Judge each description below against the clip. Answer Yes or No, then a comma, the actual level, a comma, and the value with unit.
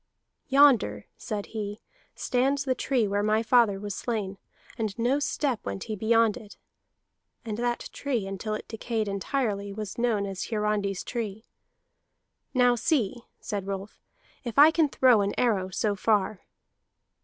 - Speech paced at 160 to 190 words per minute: No, average, 145 wpm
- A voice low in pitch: No, high, 215 Hz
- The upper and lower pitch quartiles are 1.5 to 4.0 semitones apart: Yes, average, 3.3 semitones